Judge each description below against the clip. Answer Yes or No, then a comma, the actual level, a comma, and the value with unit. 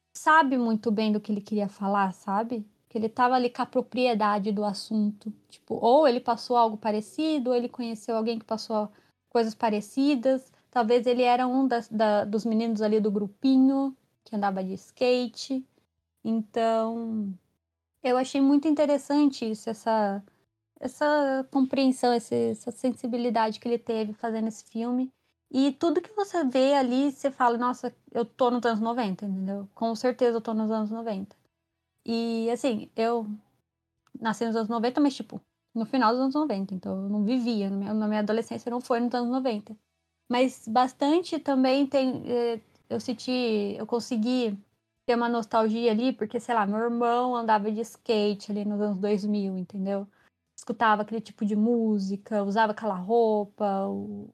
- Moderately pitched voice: No, high, 230 Hz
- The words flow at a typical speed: Yes, average, 160 wpm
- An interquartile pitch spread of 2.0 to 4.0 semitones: Yes, average, 2.9 semitones